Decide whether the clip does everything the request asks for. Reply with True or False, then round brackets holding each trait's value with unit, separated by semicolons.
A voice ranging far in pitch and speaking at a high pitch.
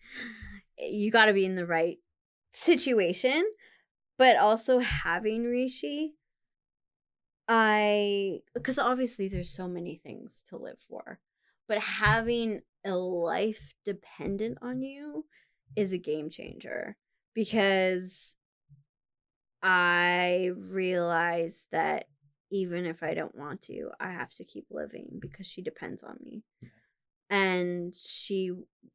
False (4.7 semitones; 195 Hz)